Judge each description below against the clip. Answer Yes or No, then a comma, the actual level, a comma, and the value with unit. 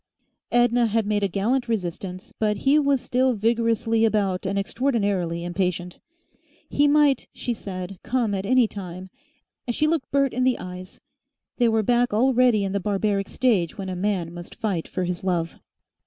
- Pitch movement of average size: Yes, average, 4.6 semitones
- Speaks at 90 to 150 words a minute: No, average, 170 wpm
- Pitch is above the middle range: Yes, high, 210 Hz